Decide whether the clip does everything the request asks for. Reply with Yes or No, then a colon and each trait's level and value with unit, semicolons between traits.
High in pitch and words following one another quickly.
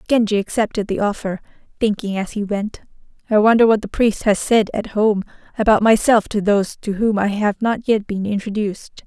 No: high, 210 Hz; average, 190 wpm